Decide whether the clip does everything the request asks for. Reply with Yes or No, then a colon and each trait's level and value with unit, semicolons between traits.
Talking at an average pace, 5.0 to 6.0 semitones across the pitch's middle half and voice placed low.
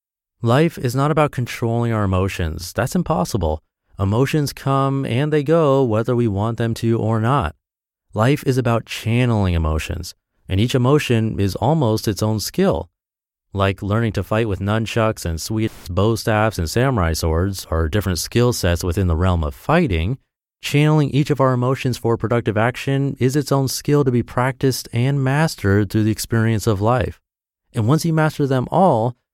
Yes: average, 170 wpm; wide, 5.4 semitones; low, 115 Hz